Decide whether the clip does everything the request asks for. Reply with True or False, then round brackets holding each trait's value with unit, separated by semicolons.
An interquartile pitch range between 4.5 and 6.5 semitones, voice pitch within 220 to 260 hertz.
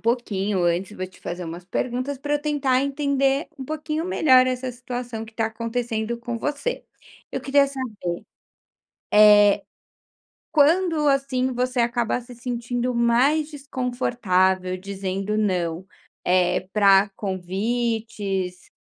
True (5.1 semitones; 235 Hz)